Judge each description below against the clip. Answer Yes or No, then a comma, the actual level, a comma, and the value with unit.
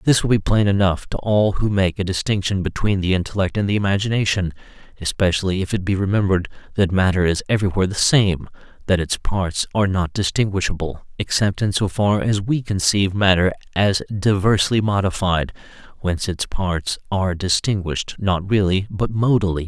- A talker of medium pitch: No, very low, 95 Hz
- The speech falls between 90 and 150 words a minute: No, average, 165 wpm